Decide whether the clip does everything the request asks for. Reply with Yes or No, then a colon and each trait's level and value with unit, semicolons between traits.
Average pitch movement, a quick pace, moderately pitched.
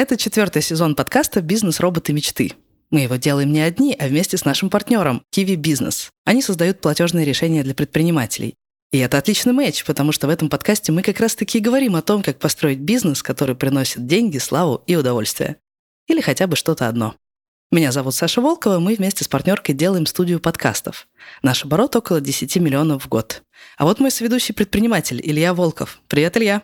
No: wide, 6.2 semitones; fast, 185 wpm; medium, 165 Hz